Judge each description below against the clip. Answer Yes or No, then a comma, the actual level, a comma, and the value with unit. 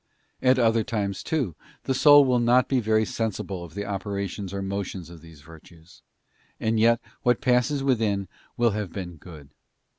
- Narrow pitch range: No, average, 4.6 semitones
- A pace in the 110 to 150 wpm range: No, average, 170 wpm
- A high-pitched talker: No, low, 105 Hz